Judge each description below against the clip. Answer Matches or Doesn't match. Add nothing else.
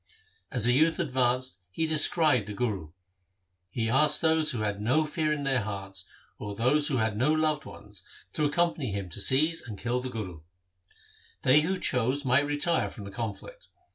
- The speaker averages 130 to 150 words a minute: Doesn't match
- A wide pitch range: Matches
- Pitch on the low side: Matches